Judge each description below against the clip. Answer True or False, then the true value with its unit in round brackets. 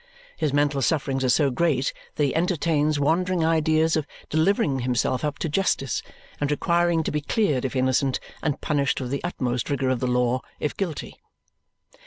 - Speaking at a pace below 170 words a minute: False (175 wpm)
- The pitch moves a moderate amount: True (3.4 semitones)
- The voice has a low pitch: False (145 Hz)